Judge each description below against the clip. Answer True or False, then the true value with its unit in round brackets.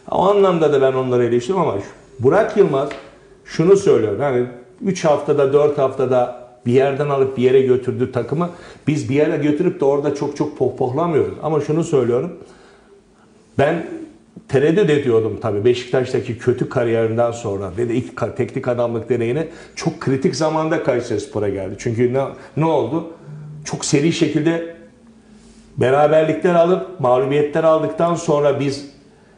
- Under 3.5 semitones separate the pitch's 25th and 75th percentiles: False (4.8 semitones)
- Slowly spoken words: False (135 wpm)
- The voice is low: False (145 Hz)